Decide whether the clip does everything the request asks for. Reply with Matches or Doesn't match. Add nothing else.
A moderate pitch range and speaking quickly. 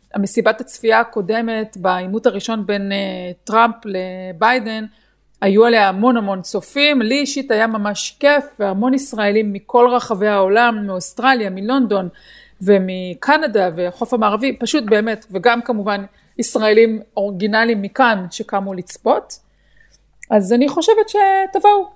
Doesn't match